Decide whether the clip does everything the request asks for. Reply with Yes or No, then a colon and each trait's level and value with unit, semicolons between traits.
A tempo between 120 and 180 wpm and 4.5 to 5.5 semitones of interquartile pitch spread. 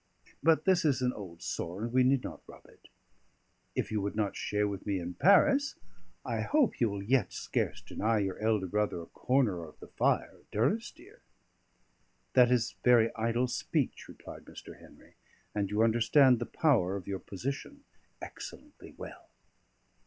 Yes: average, 165 wpm; average, 5.2 semitones